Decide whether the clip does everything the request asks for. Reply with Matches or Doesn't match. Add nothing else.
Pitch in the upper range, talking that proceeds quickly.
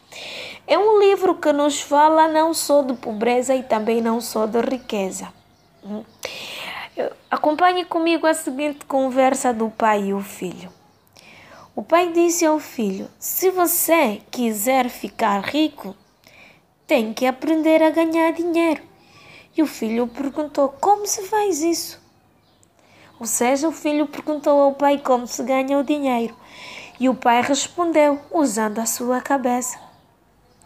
Doesn't match